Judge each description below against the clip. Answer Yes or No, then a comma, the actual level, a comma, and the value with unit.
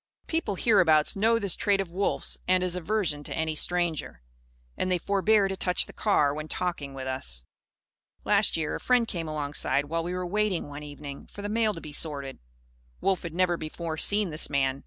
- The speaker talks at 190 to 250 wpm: Yes, average, 200 wpm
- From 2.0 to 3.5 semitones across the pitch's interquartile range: No, average, 4.8 semitones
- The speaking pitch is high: No, medium, 175 Hz